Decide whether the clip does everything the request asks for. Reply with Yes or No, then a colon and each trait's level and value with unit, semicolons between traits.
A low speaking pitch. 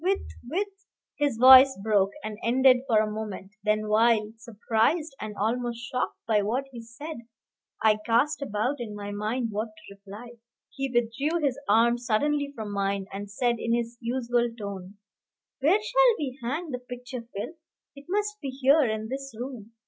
No: high, 235 Hz